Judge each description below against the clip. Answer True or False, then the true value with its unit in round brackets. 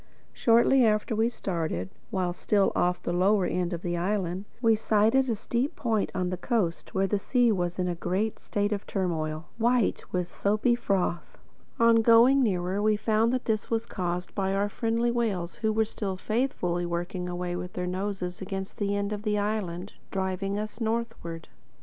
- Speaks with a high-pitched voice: True (200 Hz)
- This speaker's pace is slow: False (180 wpm)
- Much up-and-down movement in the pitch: False (3.8 semitones)